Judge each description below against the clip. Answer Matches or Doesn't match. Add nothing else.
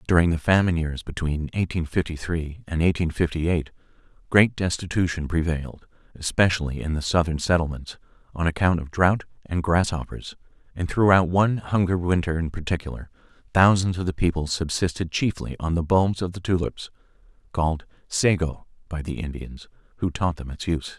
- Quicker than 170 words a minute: Doesn't match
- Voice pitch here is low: Matches